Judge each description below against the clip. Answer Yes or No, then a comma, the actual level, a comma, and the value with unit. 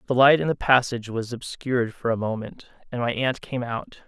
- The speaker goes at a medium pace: No, fast, 220 wpm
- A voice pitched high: No, low, 120 Hz